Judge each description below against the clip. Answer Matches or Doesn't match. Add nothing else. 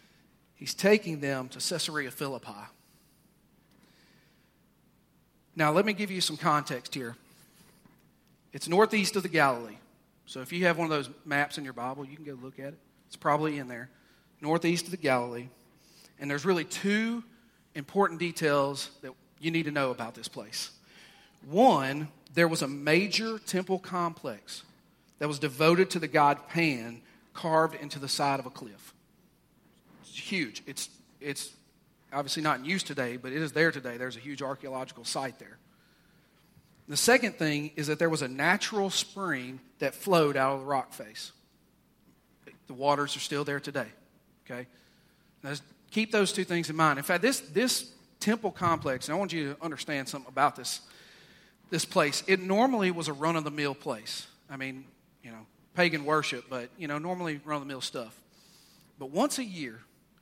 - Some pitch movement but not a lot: Matches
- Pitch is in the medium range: Matches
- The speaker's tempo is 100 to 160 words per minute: Doesn't match